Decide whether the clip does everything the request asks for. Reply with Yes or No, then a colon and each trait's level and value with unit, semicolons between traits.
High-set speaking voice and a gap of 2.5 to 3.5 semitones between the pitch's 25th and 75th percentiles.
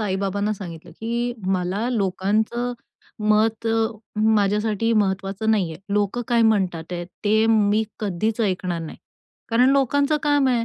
Yes: high, 215 Hz; average, 3.0 semitones